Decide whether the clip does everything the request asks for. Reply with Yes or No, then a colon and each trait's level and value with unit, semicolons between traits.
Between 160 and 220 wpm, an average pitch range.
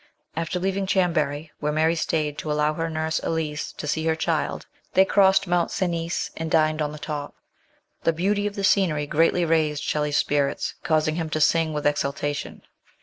No: average, 180 wpm; narrow, 2.2 semitones